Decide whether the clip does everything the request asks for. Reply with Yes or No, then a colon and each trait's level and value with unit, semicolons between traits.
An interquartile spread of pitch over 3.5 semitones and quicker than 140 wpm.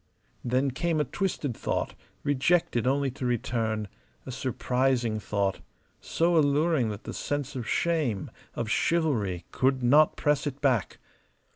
No: average, 4.2 semitones; slow, 135 wpm